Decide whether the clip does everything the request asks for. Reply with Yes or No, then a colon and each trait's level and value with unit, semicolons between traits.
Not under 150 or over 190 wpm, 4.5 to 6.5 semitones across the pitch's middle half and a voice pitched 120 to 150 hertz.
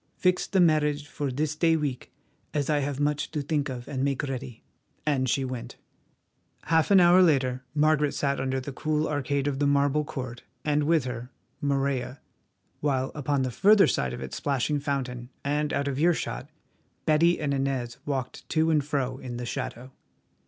No: average, 180 wpm; narrow, 2.5 semitones; medium, 140 Hz